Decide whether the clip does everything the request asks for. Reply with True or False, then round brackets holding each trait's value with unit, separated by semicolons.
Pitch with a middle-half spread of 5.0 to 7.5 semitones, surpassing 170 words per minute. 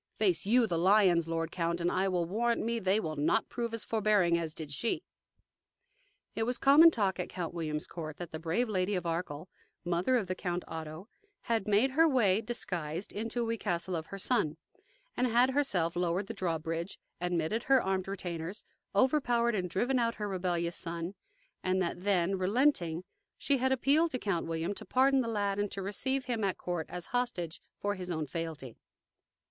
True (5.3 semitones; 185 wpm)